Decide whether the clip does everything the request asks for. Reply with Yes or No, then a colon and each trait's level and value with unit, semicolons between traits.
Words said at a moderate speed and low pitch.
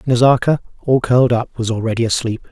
Yes: average, 165 wpm; low, 120 Hz